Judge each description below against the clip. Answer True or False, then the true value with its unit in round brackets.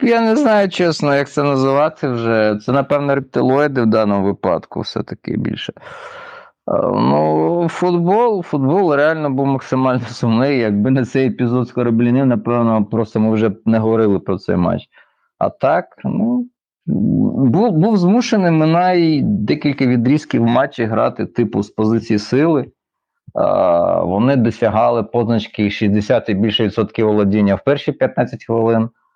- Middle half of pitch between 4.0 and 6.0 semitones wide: True (5.0 semitones)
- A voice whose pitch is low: True (125 Hz)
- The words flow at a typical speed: True (140 wpm)